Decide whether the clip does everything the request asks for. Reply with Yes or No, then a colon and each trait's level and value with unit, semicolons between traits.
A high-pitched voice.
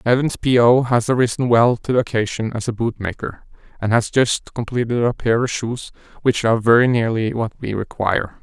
No: low, 115 Hz